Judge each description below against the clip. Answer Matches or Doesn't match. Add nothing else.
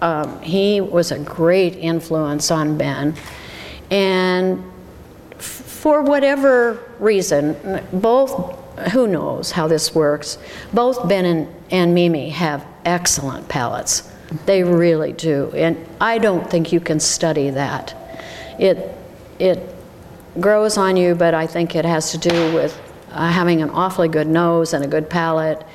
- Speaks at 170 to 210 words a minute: Doesn't match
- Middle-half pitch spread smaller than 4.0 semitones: Matches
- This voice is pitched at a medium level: Matches